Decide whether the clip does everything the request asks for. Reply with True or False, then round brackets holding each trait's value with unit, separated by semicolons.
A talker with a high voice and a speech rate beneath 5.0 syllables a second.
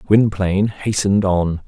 False (100 Hz; 4.7 syllables/s)